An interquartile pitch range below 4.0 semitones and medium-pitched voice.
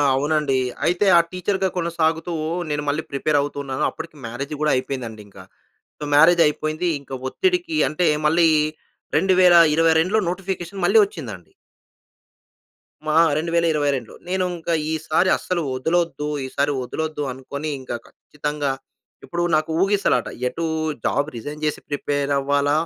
Yes: average, 3.4 semitones; medium, 155 Hz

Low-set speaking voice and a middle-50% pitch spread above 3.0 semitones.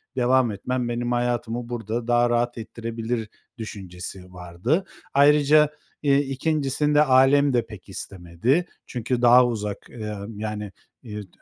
Yes: low, 120 Hz; average, 3.7 semitones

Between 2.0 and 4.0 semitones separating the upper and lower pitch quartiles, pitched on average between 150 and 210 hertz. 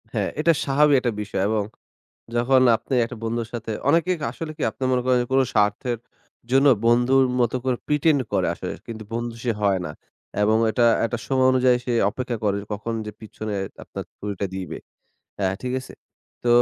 No: average, 3.1 semitones; low, 120 Hz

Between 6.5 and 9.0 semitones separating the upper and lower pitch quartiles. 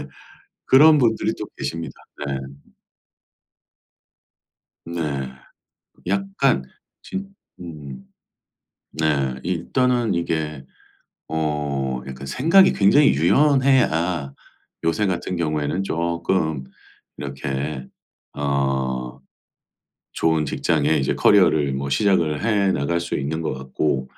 No: wide, 5.6 semitones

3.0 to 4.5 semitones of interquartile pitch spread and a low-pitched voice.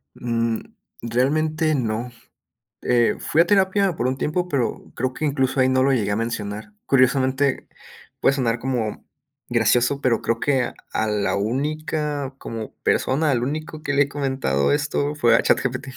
Yes: average, 3.8 semitones; low, 130 Hz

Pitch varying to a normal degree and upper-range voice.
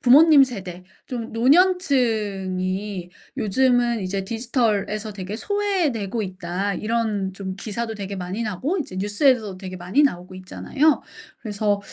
Yes: average, 4.6 semitones; high, 210 Hz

